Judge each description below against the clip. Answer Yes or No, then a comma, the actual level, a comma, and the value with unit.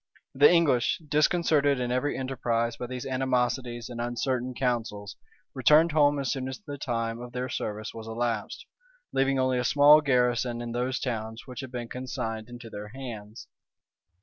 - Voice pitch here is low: Yes, low, 125 Hz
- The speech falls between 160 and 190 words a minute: Yes, average, 165 wpm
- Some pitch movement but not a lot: No, narrow, 2.3 semitones